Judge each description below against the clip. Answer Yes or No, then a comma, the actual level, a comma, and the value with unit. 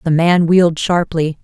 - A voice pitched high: No, medium, 165 Hz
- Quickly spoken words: No, average, 165 wpm